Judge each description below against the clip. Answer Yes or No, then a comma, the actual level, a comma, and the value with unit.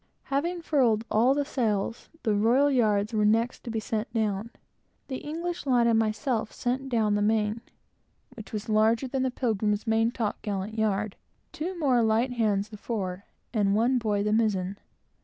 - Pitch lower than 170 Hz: No, high, 225 Hz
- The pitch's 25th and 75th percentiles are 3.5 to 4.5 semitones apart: No, average, 3.1 semitones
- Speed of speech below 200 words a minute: Yes, average, 175 wpm